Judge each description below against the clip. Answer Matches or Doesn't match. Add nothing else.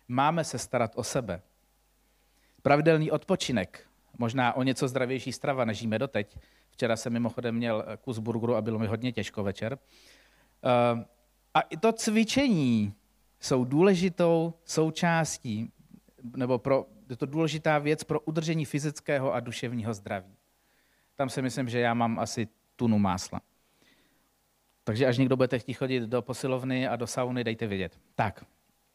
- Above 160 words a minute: Doesn't match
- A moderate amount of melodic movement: Matches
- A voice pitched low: Matches